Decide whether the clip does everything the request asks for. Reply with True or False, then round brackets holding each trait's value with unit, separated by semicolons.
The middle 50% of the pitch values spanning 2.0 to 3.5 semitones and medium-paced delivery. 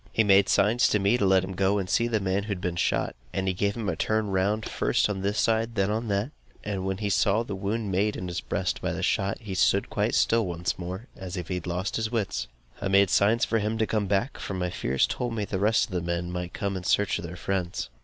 False (2.5 semitones; 275 wpm)